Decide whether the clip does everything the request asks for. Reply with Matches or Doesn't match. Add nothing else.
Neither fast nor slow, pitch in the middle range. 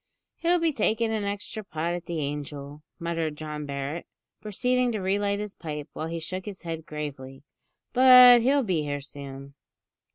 Matches